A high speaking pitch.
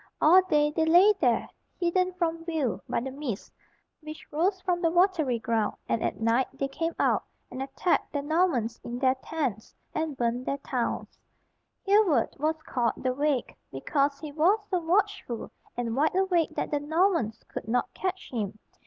Yes: very high, 295 Hz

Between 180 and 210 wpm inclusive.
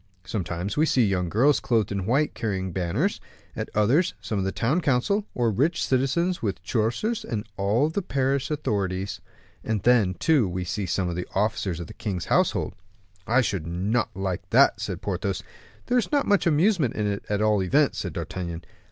Yes: average, 185 wpm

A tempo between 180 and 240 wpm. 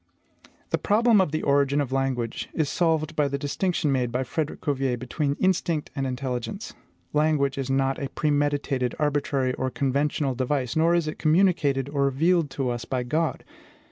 No: average, 170 wpm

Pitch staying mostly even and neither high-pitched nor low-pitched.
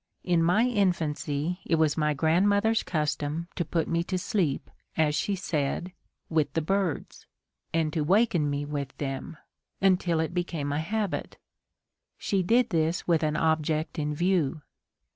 No: average, 3.4 semitones; medium, 165 Hz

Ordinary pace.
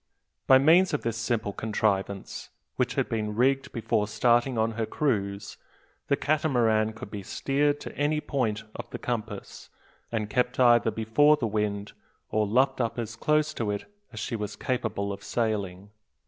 Yes: average, 165 wpm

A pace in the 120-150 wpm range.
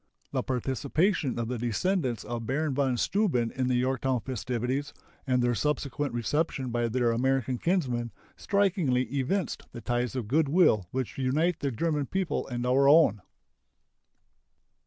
Yes: average, 145 wpm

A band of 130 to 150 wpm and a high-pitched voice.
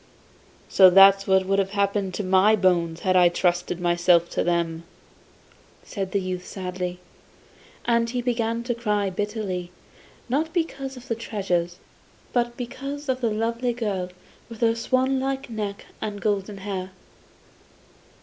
Yes: average, 140 wpm; high, 200 Hz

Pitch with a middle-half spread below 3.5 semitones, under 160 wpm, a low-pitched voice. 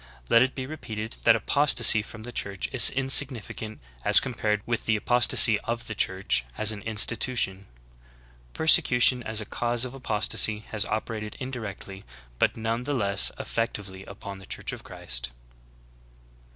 Yes: average, 2.9 semitones; average, 150 wpm; low, 110 Hz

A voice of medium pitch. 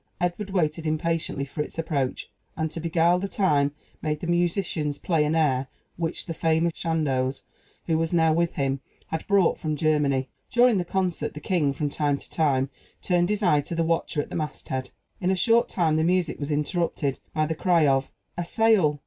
Yes: medium, 160 Hz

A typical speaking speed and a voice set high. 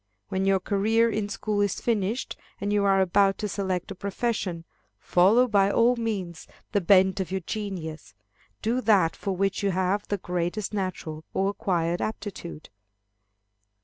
Yes: average, 155 wpm; high, 195 Hz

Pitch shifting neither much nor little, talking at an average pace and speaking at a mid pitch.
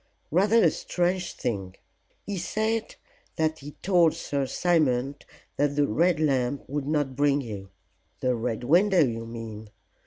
No: wide, 6.0 semitones; average, 145 wpm; medium, 145 Hz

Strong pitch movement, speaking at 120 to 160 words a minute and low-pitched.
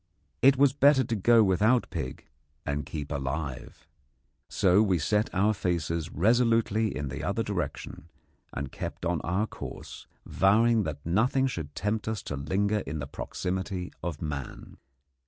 Yes: wide, 6.3 semitones; average, 150 wpm; very low, 95 Hz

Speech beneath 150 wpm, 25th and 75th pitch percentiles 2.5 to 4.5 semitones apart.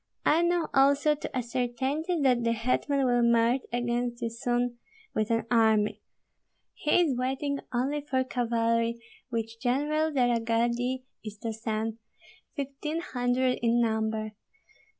Yes: average, 140 wpm; average, 2.8 semitones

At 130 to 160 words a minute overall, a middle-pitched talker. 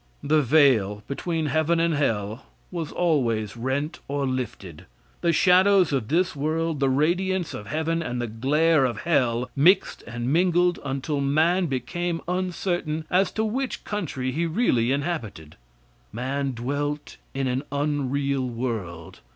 Yes: average, 140 wpm; medium, 145 Hz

